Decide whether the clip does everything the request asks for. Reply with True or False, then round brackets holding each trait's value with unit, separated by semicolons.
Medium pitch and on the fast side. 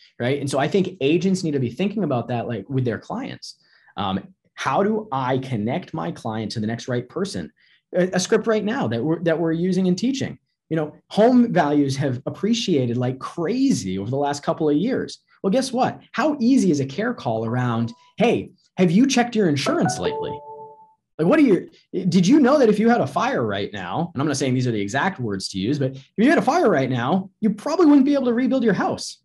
True (170 Hz; 235 wpm)